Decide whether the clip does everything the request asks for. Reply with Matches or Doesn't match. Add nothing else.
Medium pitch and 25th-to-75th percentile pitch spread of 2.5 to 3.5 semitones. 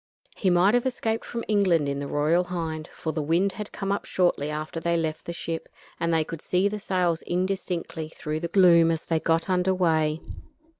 Matches